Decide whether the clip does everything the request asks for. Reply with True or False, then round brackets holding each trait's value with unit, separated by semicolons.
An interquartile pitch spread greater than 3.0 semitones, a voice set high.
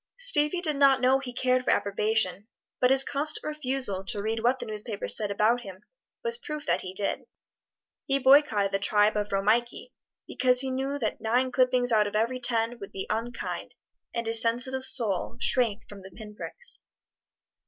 True (4.0 semitones; 235 Hz)